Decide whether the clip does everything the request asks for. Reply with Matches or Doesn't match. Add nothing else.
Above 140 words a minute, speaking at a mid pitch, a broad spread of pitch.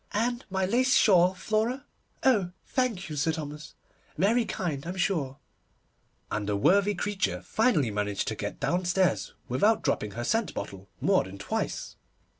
Matches